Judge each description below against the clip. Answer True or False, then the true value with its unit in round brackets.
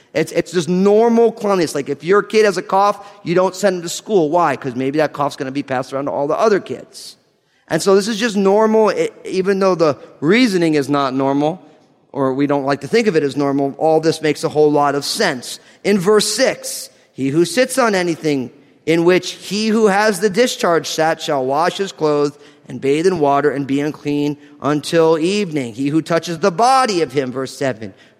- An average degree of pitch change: False (5.8 semitones)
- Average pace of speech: False (220 wpm)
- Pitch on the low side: False (160 Hz)